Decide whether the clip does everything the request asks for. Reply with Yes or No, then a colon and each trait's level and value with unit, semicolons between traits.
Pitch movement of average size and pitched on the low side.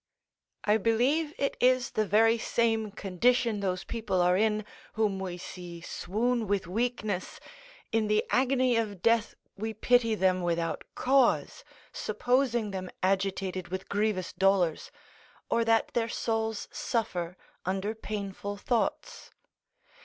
No: average, 3.5 semitones; high, 215 Hz